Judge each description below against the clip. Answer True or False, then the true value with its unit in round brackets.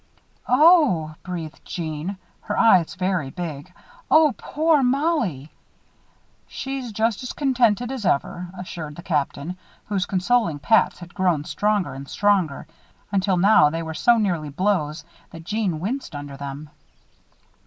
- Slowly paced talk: True (130 wpm)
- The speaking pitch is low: False (185 Hz)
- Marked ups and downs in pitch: True (6.5 semitones)